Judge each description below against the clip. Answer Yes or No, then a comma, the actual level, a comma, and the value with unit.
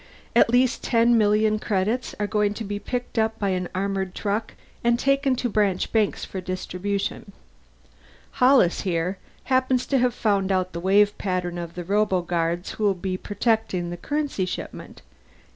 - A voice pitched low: No, high, 205 Hz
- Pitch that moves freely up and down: No, average, 3.9 semitones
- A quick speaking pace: No, average, 160 wpm